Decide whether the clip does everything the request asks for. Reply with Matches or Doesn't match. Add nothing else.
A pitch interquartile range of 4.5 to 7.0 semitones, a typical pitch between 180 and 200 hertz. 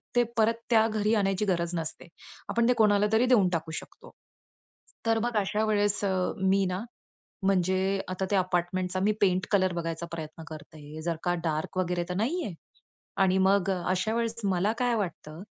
Doesn't match